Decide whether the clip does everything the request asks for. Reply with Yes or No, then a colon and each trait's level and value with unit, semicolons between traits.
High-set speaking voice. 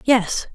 Yes: high, 230 Hz